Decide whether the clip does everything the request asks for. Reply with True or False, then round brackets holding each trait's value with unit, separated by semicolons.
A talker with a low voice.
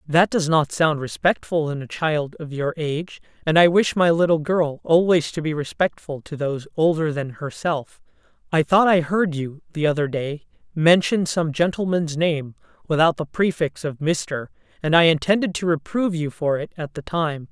False (160 Hz)